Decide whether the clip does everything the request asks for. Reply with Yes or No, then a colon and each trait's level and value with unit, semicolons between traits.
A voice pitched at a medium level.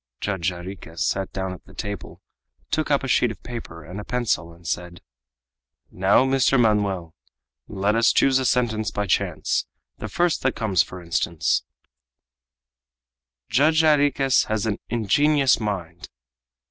No: low, 105 Hz